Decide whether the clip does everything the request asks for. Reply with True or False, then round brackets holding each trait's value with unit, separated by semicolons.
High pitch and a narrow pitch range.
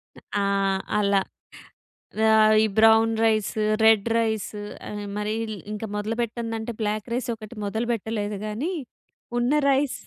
True (220 Hz; 1.4 semitones)